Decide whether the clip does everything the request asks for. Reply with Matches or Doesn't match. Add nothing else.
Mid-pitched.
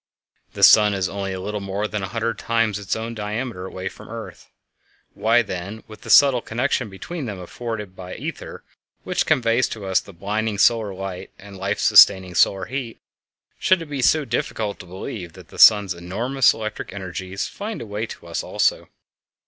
Doesn't match